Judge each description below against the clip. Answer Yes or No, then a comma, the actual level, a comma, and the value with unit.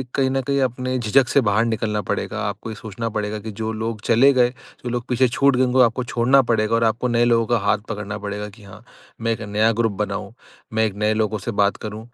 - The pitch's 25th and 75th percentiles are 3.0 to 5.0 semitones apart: No, narrow, 2.4 semitones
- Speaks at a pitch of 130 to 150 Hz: No, low, 115 Hz